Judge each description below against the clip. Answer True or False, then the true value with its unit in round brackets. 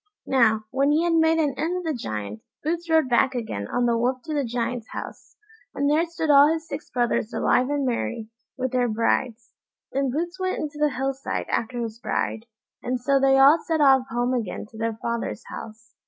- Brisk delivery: True (210 wpm)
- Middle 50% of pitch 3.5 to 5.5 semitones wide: True (4.3 semitones)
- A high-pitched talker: True (260 Hz)